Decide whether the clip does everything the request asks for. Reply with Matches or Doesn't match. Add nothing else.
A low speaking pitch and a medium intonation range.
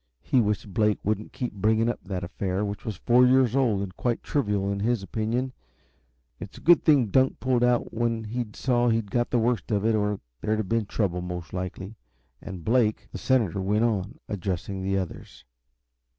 Matches